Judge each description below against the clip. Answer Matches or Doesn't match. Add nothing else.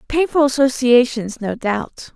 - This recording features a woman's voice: Matches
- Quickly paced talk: Doesn't match